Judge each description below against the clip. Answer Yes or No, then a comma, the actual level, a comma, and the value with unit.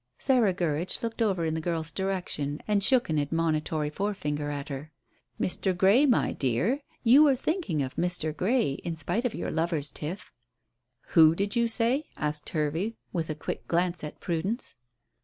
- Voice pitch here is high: No, medium, 170 Hz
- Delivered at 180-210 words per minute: No, average, 170 wpm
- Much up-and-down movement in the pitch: Yes, wide, 6.1 semitones